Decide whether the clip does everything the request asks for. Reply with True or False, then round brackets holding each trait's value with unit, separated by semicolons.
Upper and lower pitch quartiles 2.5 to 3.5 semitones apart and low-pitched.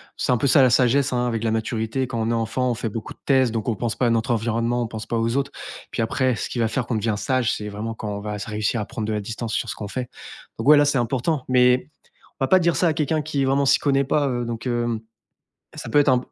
True (2.9 semitones; 120 Hz)